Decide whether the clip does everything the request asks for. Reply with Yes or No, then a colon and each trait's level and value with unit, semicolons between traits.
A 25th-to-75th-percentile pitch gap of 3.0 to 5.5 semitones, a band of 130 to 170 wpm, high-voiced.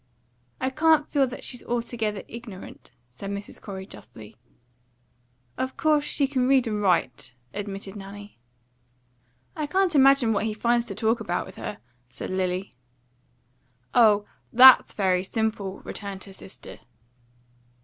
Yes: average, 4.8 semitones; slow, 135 wpm; high, 215 Hz